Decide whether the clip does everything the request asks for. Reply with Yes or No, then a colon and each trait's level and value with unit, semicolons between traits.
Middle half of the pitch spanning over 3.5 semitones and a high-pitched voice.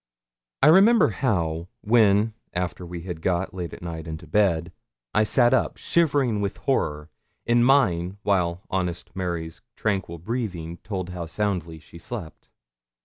No: average, 4.2 semitones; very low, 90 Hz